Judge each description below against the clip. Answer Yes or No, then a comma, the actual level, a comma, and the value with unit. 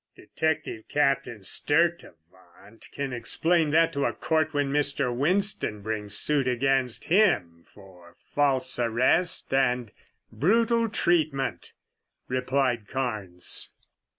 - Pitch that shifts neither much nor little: No, wide, 5.9 semitones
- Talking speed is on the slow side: Yes, slow, 100 wpm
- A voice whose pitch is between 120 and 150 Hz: Yes, low, 135 Hz